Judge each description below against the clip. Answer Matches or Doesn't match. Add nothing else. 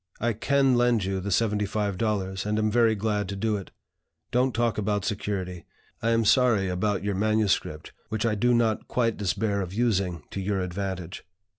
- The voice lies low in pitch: Matches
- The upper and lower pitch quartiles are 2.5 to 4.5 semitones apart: Matches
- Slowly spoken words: Doesn't match